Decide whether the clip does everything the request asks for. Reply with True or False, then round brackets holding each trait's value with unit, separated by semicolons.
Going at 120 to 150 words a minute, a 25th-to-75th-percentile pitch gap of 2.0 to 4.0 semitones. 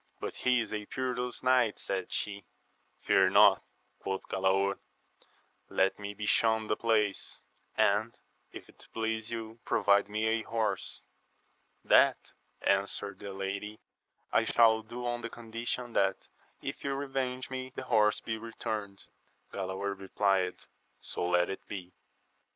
True (140 wpm; 2.9 semitones)